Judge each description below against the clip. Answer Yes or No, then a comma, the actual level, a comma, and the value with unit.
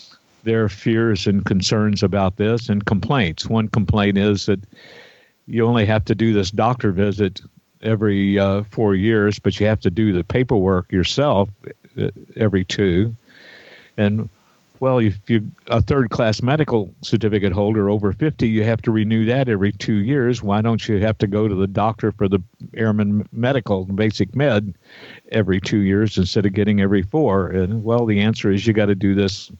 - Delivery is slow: No, average, 175 wpm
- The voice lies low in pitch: Yes, low, 105 Hz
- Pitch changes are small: Yes, narrow, 2.0 semitones